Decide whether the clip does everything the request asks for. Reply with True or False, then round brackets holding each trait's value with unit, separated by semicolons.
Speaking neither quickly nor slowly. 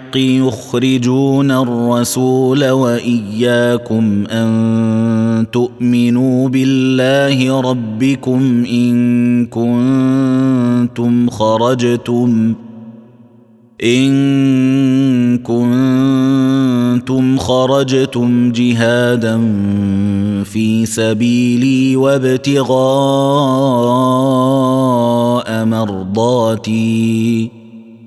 False (40 wpm)